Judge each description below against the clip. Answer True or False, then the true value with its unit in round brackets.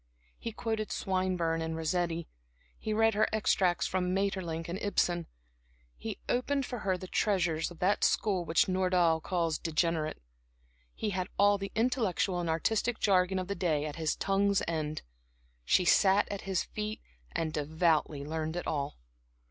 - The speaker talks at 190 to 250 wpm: False (155 wpm)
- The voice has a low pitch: False (180 Hz)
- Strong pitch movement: False (3.6 semitones)